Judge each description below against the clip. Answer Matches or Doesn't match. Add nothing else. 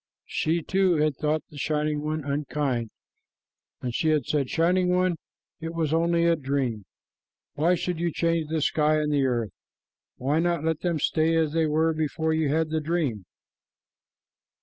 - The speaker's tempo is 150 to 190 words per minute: Matches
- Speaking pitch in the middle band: Matches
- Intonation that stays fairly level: Matches